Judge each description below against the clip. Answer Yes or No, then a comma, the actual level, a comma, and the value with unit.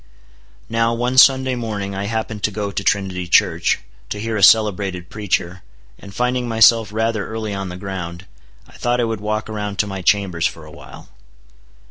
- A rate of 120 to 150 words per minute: No, average, 180 wpm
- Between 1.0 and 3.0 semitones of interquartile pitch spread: Yes, average, 2.7 semitones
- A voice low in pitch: Yes, low, 105 Hz